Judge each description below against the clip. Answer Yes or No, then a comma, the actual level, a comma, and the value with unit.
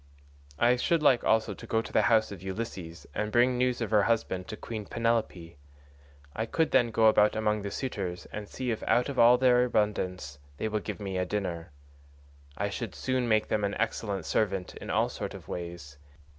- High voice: No, low, 110 Hz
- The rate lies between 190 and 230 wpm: Yes, average, 200 wpm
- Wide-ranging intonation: No, average, 3.8 semitones